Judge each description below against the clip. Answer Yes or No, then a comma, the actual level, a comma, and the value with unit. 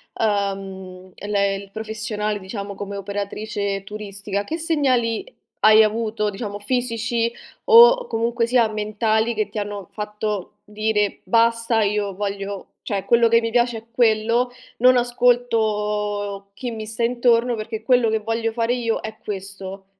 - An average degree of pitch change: No, narrow, 2.3 semitones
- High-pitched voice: Yes, high, 215 Hz